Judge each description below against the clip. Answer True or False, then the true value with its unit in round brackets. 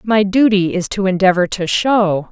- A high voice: True (195 Hz)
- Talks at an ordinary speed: True (180 wpm)